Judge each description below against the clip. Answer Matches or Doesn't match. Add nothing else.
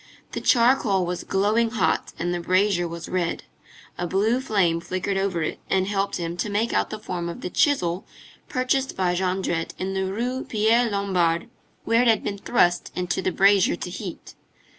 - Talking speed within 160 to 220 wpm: Matches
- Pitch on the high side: Matches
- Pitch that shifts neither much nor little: Matches